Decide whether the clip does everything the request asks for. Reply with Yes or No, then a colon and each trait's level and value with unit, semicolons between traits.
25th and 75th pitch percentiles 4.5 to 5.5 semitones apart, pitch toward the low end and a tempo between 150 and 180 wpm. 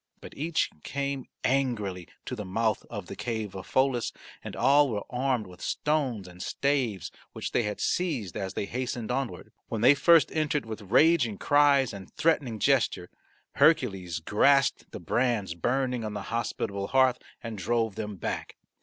Yes: average, 5.0 semitones; low, 120 Hz; average, 165 wpm